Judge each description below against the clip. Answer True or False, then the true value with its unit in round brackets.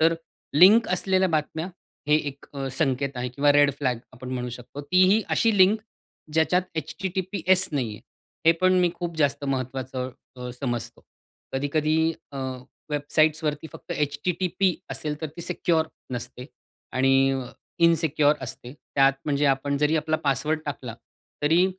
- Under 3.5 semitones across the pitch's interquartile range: False (3.9 semitones)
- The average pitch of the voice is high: False (150 Hz)